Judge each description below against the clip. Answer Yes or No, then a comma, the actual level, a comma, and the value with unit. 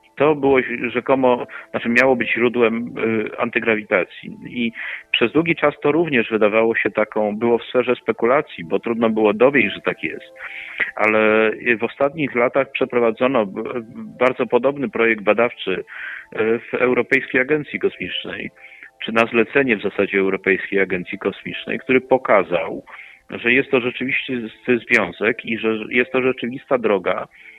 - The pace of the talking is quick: No, average, 135 wpm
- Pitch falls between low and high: No, low, 120 Hz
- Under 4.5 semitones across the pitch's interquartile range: Yes, narrow, 2.6 semitones